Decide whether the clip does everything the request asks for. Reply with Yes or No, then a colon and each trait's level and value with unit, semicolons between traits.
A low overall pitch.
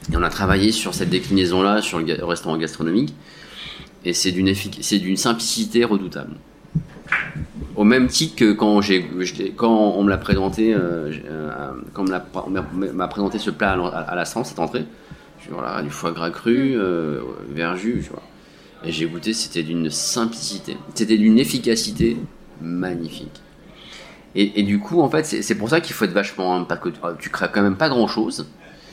Yes: very low, 95 Hz